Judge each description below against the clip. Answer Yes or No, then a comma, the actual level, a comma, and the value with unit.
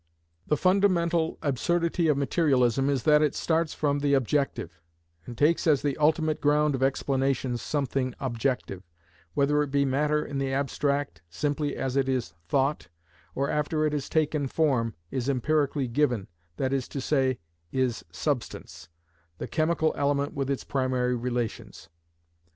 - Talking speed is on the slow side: No, average, 145 wpm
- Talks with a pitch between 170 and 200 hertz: No, medium, 140 Hz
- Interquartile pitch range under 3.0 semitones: Yes, narrow, 2.6 semitones